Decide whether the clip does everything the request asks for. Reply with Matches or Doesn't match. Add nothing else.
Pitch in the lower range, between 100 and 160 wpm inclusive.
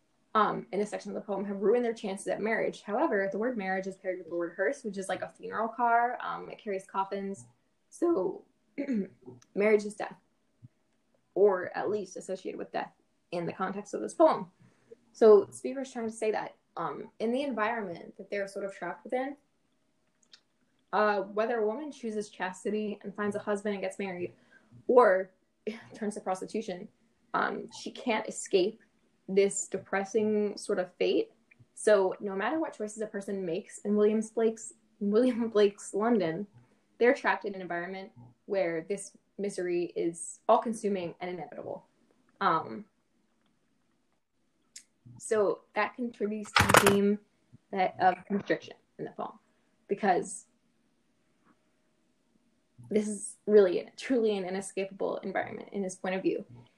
Doesn't match